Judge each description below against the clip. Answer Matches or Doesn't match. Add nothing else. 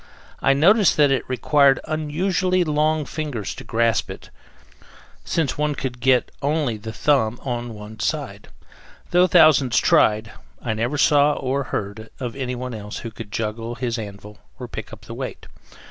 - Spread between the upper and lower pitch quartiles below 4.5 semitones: Doesn't match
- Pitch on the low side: Matches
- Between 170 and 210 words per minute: Doesn't match